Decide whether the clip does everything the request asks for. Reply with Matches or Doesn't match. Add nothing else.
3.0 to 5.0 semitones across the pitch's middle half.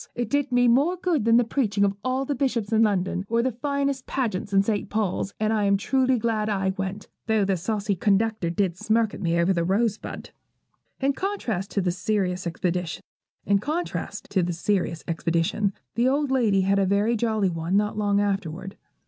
Matches